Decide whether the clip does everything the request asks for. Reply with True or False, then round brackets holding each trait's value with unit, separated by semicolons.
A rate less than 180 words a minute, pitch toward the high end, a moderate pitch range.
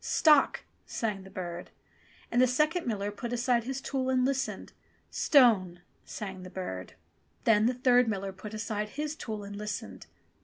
True (165 wpm; 220 Hz; 4.4 semitones)